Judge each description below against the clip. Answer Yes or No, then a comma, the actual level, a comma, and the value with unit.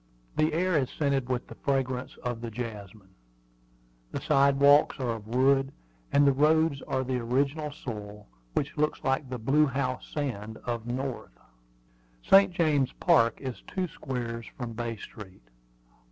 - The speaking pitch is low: Yes, low, 130 Hz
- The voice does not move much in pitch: No, average, 3.5 semitones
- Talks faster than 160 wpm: No, average, 155 wpm